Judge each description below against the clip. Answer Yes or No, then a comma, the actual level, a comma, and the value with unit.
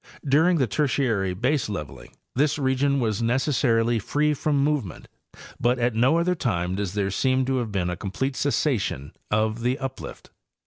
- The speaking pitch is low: Yes, low, 125 Hz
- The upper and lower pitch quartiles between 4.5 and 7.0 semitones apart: Yes, average, 5.1 semitones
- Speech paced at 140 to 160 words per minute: Yes, average, 155 wpm